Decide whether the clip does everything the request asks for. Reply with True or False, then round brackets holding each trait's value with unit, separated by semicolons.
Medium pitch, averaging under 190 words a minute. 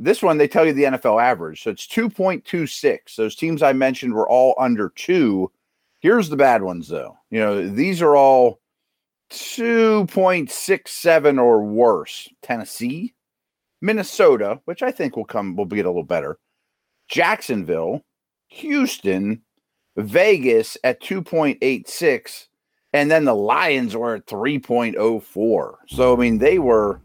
True (155 Hz; 135 wpm)